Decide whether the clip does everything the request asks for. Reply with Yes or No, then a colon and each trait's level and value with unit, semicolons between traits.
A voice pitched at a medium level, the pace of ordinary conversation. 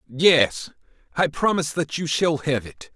Yes: medium, 150 Hz; average, 165 wpm